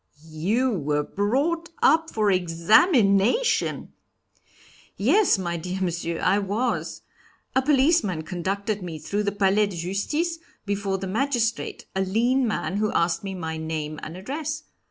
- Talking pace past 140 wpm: No, slow, 135 wpm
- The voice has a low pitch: No, high, 200 Hz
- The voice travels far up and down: Yes, wide, 6.2 semitones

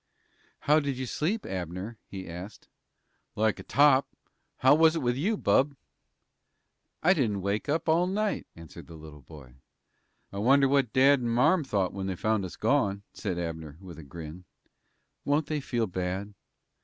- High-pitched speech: No, low, 110 Hz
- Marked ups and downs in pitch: Yes, wide, 7.6 semitones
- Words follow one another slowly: No, average, 165 wpm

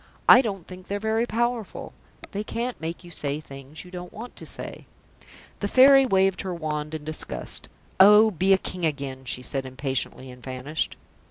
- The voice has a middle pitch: Yes, medium, 180 Hz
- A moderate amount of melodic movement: No, wide, 6.5 semitones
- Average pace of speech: Yes, average, 180 wpm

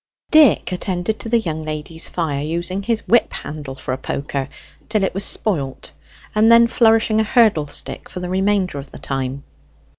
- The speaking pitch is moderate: Yes, medium, 180 Hz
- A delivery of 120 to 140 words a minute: No, average, 180 wpm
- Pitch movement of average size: No, wide, 6.8 semitones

